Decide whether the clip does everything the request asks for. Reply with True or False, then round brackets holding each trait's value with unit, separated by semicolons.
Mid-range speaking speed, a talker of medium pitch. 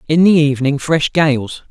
True (175 wpm; 150 Hz)